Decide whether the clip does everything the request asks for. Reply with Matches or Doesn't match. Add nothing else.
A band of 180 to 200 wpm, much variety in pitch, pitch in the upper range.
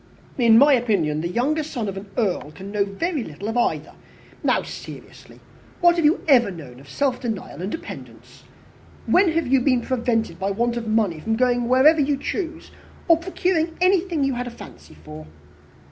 Matches